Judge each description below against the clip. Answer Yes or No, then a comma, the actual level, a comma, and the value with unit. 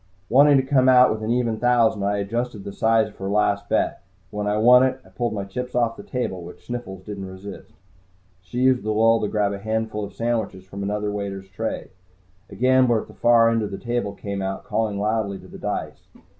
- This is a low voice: Yes, low, 110 Hz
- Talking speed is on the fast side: Yes, fast, 225 wpm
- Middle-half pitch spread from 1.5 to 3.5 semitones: Yes, average, 3.2 semitones